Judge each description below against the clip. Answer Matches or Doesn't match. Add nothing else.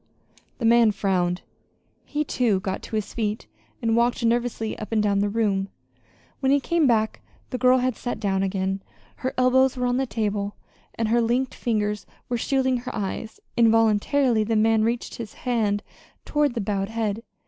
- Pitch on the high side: Matches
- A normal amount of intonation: Matches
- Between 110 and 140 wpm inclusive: Doesn't match